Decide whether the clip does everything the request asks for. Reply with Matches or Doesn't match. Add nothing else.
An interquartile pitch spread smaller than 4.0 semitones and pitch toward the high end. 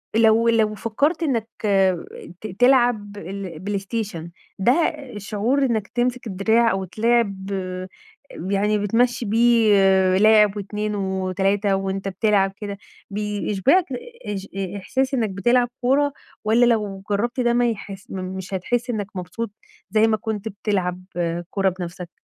Matches